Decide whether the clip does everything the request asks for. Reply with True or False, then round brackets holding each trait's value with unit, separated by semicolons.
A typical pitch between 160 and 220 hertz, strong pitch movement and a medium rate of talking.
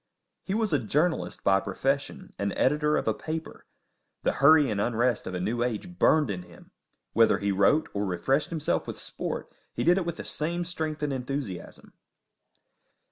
False (135 Hz; 7.1 semitones; 180 wpm)